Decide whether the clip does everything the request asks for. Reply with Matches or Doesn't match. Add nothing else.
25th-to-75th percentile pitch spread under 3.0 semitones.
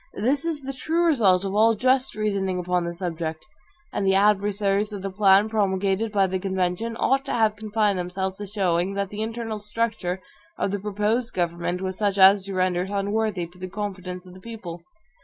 Matches